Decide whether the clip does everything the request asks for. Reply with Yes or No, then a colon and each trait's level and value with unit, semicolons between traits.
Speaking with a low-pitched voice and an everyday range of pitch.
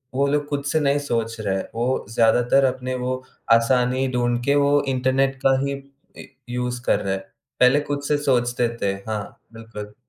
Yes: low, 125 Hz; average, 3.1 semitones